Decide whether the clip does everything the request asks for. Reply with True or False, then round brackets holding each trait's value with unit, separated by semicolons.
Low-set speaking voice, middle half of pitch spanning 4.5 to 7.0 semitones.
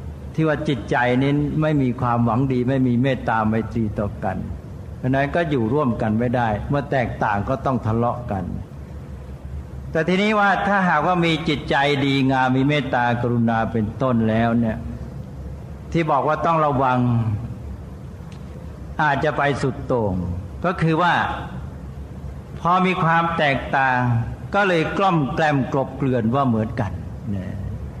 True (125 Hz; 5.2 semitones)